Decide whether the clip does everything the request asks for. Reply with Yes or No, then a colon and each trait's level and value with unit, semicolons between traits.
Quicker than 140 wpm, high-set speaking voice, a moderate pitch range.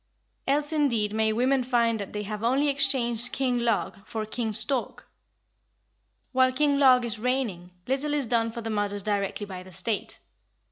Yes: average, 170 wpm; high, 235 Hz; average, 3.9 semitones